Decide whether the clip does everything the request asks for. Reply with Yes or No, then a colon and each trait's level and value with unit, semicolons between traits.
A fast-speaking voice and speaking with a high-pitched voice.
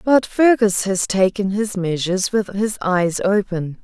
No: average, 155 wpm; high, 200 Hz